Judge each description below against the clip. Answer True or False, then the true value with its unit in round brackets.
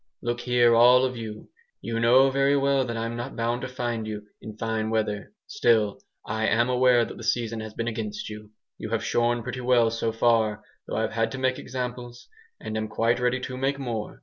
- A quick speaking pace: True (210 wpm)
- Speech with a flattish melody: True (2.1 semitones)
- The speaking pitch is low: True (120 Hz)